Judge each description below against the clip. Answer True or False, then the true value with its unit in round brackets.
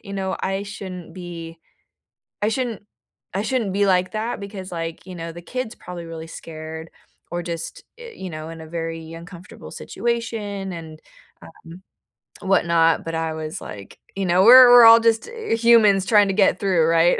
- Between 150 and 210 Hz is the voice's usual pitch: True (185 Hz)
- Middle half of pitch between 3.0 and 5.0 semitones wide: True (4.1 semitones)